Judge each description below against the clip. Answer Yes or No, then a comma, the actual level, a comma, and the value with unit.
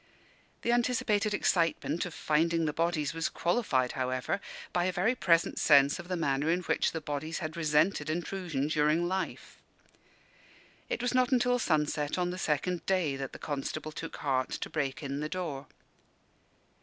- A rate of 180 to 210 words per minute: No, average, 165 wpm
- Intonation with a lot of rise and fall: No, average, 3.7 semitones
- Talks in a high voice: No, medium, 165 Hz